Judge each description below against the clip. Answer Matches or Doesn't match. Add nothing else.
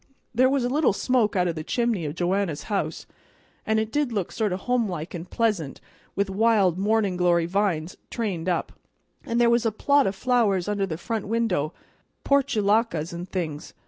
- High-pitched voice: Matches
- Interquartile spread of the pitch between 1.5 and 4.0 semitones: Doesn't match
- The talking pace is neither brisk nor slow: Matches